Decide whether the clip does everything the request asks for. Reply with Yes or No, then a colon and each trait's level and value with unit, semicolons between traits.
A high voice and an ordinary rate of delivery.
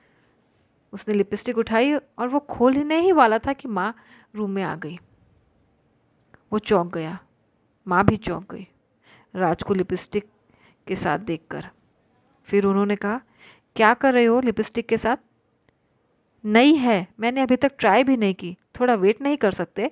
Yes: high, 210 Hz; average, 155 wpm